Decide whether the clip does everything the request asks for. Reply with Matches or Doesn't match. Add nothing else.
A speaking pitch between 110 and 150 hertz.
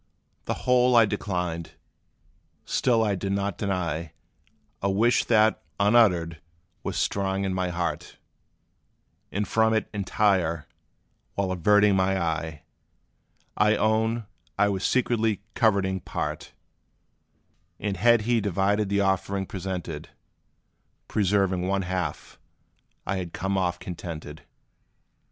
Doesn't match